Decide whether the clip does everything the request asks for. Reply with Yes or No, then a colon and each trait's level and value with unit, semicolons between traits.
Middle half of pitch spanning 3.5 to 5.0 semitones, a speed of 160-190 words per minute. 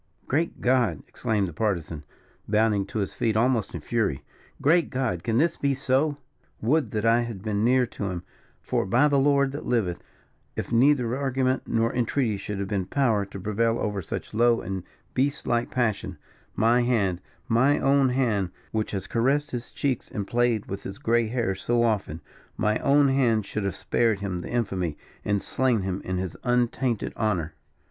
Yes: average, 4.3 semitones; average, 180 wpm